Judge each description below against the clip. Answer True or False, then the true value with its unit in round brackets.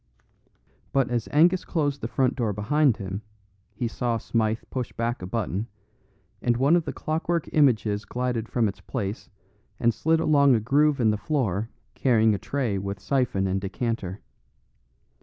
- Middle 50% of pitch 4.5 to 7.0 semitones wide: True (4.9 semitones)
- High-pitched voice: False (120 Hz)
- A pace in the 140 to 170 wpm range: True (160 wpm)